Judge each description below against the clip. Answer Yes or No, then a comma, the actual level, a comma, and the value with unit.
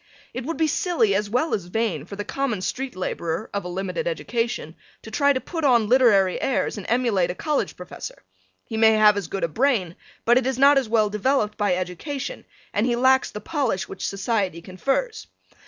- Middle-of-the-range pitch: No, high, 225 Hz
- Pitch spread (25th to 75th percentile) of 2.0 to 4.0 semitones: No, wide, 5.4 semitones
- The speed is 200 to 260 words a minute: Yes, fast, 205 wpm